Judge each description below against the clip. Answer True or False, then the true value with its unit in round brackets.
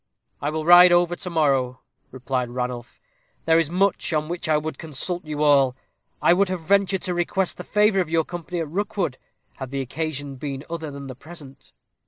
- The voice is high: False (155 Hz)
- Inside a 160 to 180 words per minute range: False (195 wpm)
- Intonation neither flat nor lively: True (4.3 semitones)